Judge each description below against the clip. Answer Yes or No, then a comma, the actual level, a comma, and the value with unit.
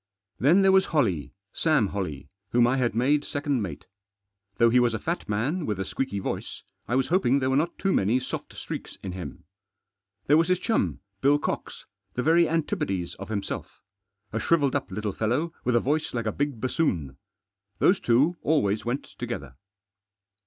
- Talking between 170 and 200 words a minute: Yes, average, 180 wpm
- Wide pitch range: Yes, wide, 6.6 semitones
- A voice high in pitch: No, low, 125 Hz